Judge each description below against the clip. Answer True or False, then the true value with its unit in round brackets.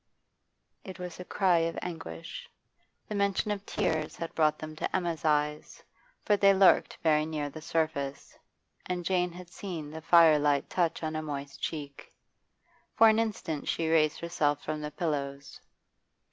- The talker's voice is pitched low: False (160 Hz)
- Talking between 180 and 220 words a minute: False (160 wpm)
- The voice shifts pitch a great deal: False (3.0 semitones)